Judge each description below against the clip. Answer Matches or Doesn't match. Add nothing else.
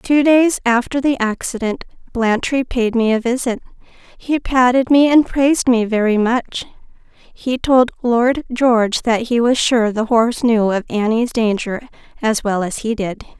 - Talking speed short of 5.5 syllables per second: Matches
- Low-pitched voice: Doesn't match